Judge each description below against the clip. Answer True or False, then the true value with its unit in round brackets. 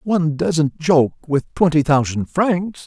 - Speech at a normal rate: True (145 wpm)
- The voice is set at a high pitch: False (160 Hz)